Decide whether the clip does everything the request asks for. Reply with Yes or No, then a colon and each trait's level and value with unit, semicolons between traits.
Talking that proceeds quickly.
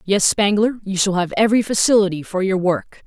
No: average, 195 wpm